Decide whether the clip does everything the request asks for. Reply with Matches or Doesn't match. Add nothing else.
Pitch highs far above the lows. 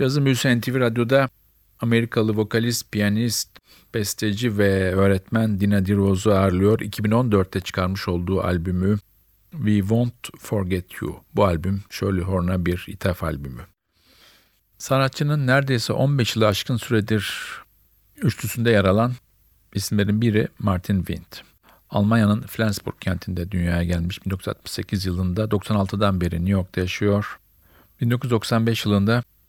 Doesn't match